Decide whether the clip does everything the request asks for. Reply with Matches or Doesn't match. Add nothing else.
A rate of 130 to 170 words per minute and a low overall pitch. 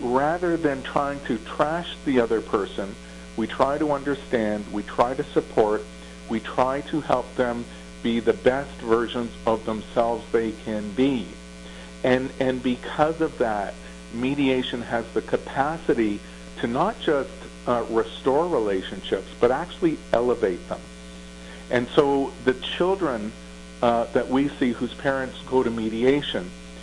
Matches